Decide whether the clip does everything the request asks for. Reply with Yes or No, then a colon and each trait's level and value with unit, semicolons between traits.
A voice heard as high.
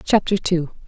No: medium, 180 Hz